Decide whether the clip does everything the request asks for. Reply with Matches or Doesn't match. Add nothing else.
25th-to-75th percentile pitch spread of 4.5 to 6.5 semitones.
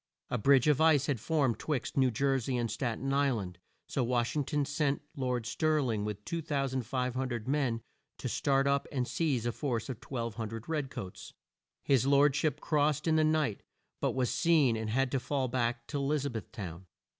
Doesn't match